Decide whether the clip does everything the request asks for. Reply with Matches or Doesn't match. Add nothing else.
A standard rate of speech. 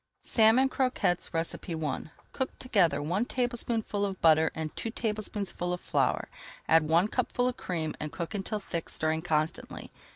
Matches